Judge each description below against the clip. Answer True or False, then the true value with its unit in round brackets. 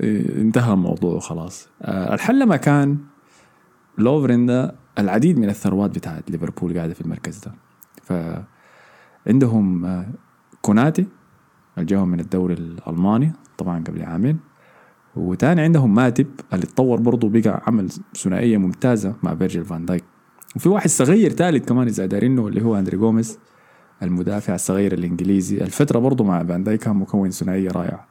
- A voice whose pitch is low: True (105 Hz)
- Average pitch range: False (6.2 semitones)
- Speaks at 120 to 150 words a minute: True (135 wpm)